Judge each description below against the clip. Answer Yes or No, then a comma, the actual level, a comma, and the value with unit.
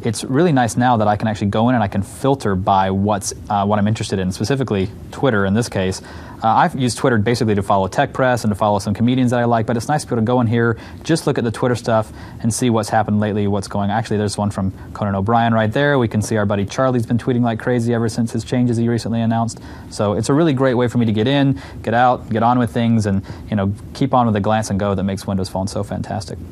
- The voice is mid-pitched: No, low, 110 Hz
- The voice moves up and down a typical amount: Yes, average, 3.2 semitones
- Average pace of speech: No, fast, 280 wpm